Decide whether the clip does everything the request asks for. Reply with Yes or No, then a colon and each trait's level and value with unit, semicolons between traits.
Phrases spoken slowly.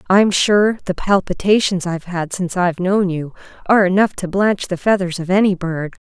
No: average, 190 wpm